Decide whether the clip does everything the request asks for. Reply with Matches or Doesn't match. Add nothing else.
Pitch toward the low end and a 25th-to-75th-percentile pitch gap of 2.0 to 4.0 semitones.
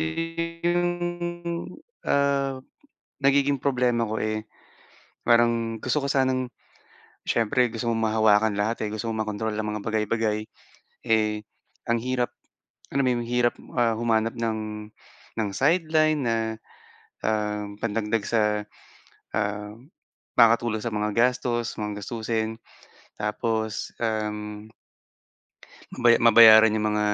Matches